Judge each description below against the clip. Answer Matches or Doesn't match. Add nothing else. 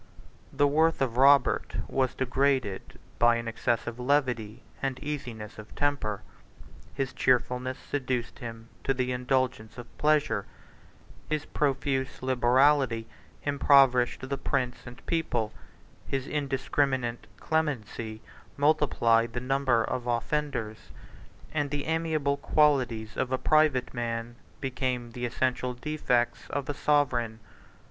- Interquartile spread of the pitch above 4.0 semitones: Doesn't match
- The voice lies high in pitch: Doesn't match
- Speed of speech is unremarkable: Doesn't match